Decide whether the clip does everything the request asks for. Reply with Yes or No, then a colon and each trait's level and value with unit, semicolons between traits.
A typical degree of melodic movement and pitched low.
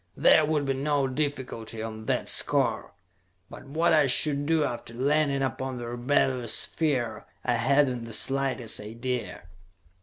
Yes: average, 3.2 semitones; low, 130 Hz